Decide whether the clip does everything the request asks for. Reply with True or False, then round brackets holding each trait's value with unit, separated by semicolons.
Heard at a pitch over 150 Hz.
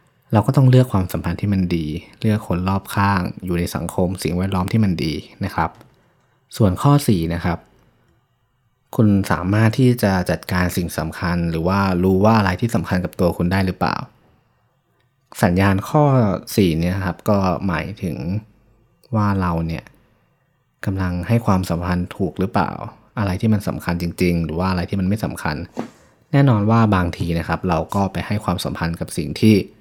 False (95 Hz)